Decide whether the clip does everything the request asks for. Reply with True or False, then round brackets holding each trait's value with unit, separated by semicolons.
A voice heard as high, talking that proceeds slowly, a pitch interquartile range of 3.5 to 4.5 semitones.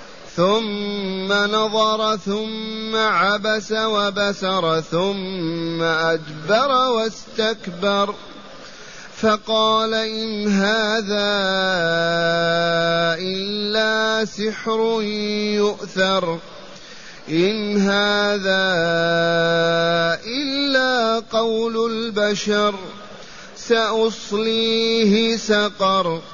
False (205 Hz; 50 wpm; 2.8 semitones)